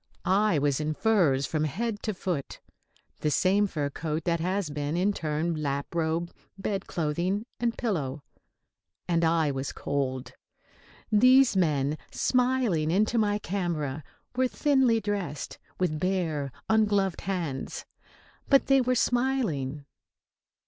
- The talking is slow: Yes, slow, 130 wpm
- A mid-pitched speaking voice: Yes, medium, 175 Hz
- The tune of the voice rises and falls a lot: Yes, wide, 5.8 semitones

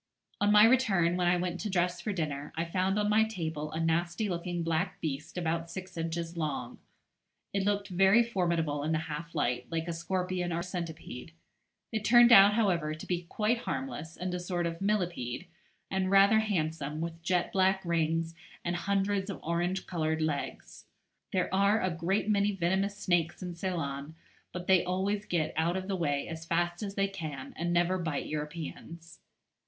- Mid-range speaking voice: Yes, medium, 175 Hz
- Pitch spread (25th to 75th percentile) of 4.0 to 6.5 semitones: No, average, 2.9 semitones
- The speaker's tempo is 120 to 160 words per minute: No, average, 180 wpm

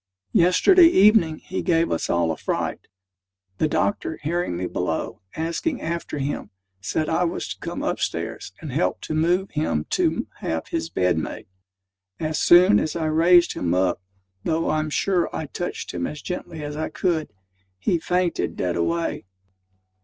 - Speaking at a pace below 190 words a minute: Yes, average, 165 wpm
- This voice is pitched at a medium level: Yes, medium, 155 Hz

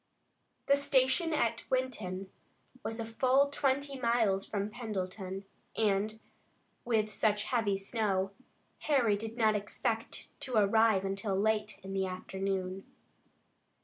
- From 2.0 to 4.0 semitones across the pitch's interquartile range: Yes, average, 3.7 semitones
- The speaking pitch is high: Yes, high, 215 Hz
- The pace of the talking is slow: Yes, slow, 115 wpm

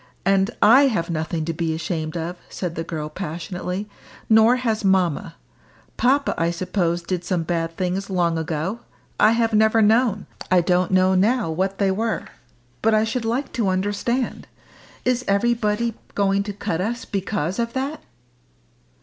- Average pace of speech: Yes, average, 160 wpm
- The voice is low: No, high, 195 Hz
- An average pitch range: Yes, average, 4.6 semitones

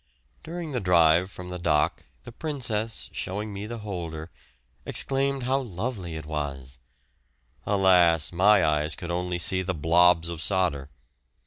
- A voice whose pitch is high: No, very low, 90 Hz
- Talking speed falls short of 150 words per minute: Yes, average, 140 wpm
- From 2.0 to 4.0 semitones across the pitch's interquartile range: No, average, 4.5 semitones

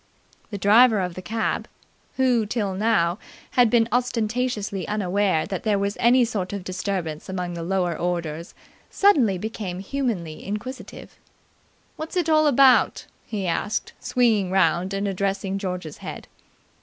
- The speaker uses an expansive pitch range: No, average, 4.3 semitones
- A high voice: Yes, high, 200 Hz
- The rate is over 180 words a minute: No, average, 140 wpm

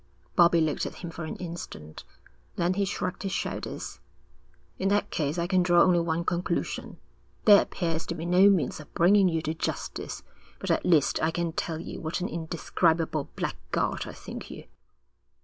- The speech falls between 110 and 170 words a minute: No, average, 180 wpm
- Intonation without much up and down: Yes, narrow, 2.1 semitones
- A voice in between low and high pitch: Yes, medium, 170 Hz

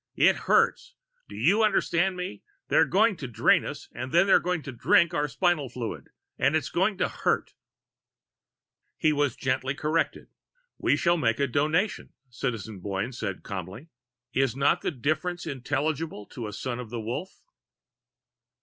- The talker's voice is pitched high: No, medium, 140 Hz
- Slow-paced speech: No, average, 160 wpm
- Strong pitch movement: Yes, wide, 6.2 semitones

